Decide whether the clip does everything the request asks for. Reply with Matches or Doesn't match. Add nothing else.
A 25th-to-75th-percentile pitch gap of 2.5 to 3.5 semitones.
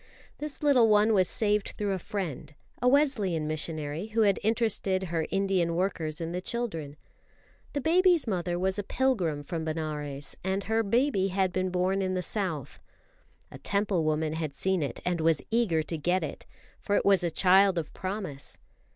Doesn't match